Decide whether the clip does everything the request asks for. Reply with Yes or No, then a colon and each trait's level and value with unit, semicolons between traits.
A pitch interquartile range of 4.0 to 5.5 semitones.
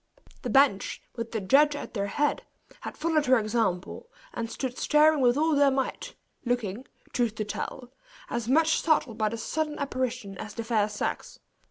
Yes: average, 4.9 semitones